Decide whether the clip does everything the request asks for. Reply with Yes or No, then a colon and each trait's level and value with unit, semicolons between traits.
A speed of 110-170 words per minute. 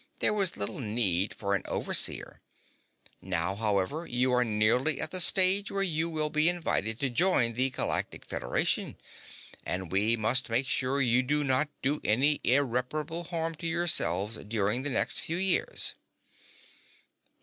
Yes: average, 150 wpm